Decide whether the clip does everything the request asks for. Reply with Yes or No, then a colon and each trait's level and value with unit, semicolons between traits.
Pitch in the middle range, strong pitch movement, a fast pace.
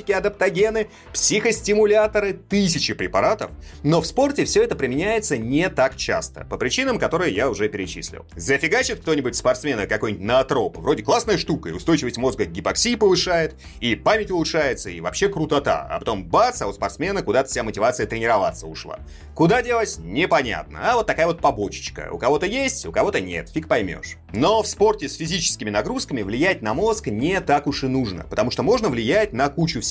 Yes: medium, 180 Hz; wide, 8.5 semitones; fast, 175 wpm